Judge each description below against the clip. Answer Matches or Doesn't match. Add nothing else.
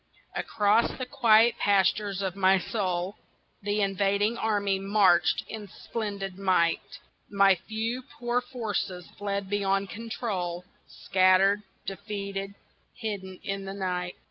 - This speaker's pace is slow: Matches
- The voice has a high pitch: Matches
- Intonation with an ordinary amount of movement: Doesn't match